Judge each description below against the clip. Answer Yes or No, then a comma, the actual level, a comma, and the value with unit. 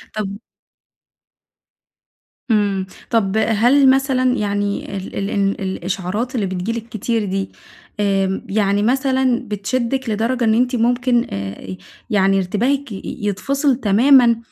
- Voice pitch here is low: No, high, 220 Hz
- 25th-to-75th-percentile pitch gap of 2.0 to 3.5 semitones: No, average, 4.2 semitones